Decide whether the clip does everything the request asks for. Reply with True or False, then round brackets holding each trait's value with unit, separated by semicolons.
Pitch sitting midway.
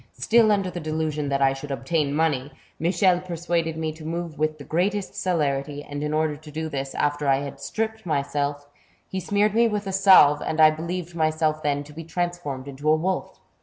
True (155 Hz)